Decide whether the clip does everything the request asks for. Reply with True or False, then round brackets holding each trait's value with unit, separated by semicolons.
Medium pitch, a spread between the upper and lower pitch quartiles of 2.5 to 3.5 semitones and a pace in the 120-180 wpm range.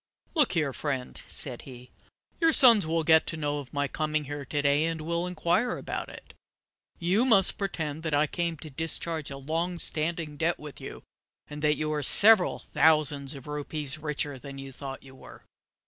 False (155 Hz; 2.9 semitones; 190 wpm)